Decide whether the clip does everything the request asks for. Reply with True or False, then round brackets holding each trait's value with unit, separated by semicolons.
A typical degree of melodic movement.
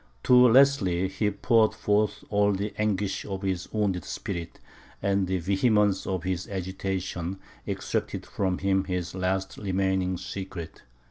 False (1.8 semitones)